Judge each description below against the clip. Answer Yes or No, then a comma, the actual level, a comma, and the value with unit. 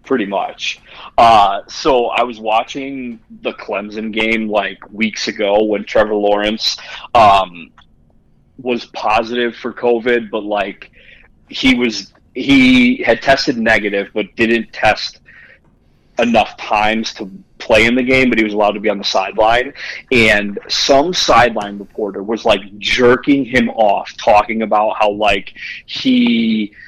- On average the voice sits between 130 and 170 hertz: No, low, 110 Hz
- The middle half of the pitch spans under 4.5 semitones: Yes, average, 2.7 semitones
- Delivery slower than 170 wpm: Yes, average, 140 wpm